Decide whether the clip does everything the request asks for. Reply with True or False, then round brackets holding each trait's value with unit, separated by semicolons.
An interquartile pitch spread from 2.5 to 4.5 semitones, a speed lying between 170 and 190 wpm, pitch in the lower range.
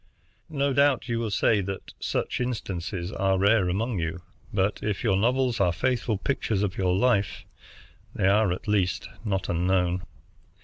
False (4.0 semitones; 160 wpm; 100 Hz)